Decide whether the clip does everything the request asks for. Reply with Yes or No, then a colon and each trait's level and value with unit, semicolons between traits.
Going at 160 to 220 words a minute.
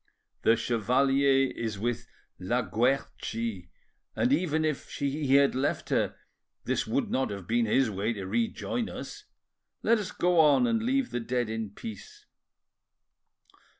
No: average, 145 wpm